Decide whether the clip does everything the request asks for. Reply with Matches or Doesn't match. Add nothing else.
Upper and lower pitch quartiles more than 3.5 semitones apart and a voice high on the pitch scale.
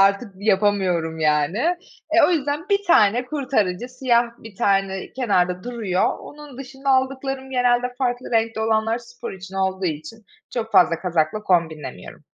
Matches